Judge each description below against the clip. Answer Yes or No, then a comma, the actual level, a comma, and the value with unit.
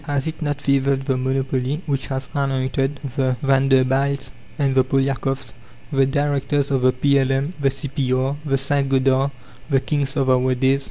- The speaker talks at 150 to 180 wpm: Yes, average, 160 wpm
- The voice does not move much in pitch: Yes, narrow, 1.1 semitones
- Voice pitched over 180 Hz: No, low, 135 Hz